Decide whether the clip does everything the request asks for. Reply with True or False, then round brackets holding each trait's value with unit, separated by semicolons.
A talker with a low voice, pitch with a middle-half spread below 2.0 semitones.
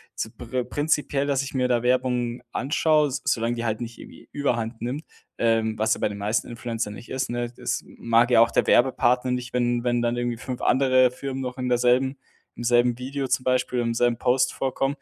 True (125 Hz; 1.6 semitones)